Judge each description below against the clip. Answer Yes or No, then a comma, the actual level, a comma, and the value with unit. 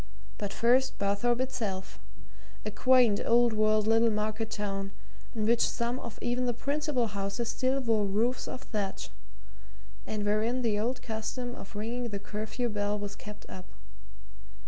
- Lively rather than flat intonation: No, average, 2.7 semitones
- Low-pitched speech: No, high, 220 Hz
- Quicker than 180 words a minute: No, average, 150 wpm